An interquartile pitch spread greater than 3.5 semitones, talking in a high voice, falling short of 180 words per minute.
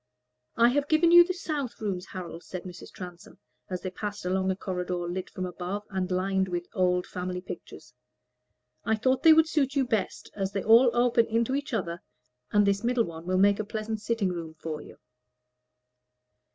No: average, 4.6 semitones; high, 195 Hz; average, 190 wpm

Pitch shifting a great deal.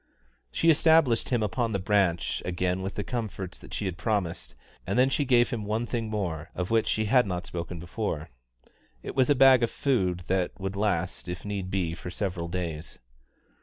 No: average, 4.7 semitones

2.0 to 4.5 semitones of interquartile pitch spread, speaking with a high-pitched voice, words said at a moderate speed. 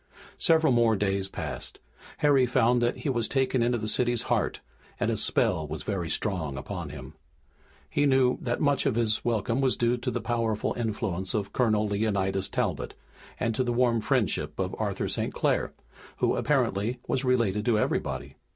No: average, 3.3 semitones; low, 115 Hz; average, 175 wpm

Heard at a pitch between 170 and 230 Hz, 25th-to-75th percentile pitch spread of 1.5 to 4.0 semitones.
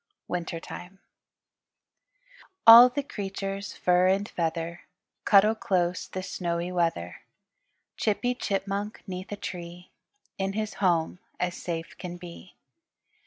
Yes: medium, 185 Hz; narrow, 2.5 semitones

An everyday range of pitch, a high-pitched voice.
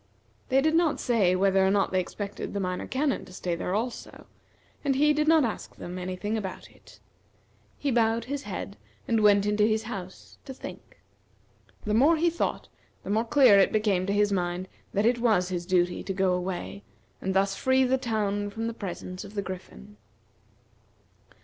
Yes: average, 4.4 semitones; high, 205 Hz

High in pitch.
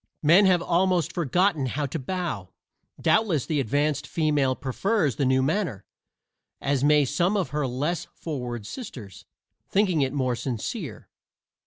No: medium, 150 Hz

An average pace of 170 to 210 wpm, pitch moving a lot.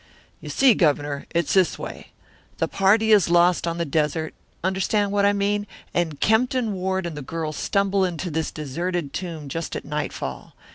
No: average, 175 wpm; average, 4.2 semitones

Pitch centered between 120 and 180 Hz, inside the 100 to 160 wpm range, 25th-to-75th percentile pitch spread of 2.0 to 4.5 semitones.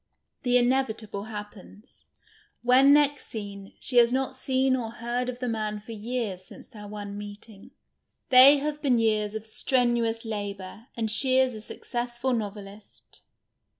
No: high, 230 Hz; average, 150 wpm; average, 3.4 semitones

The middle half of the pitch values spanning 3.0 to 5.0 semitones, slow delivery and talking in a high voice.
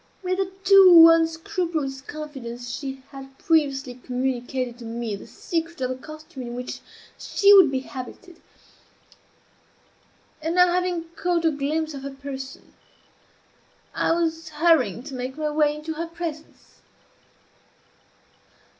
Yes: average, 4.0 semitones; slow, 130 wpm; very high, 300 Hz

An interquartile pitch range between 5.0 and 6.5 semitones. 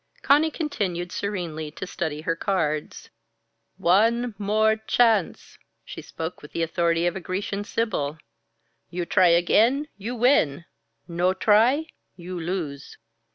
No: average, 4.6 semitones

